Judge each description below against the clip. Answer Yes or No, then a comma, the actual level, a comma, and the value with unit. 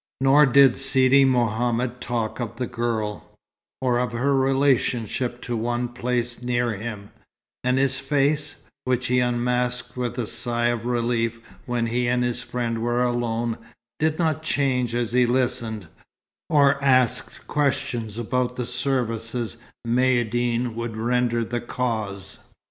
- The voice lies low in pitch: Yes, low, 120 Hz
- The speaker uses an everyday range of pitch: No, narrow, 1.5 semitones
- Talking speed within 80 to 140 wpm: Yes, slow, 135 wpm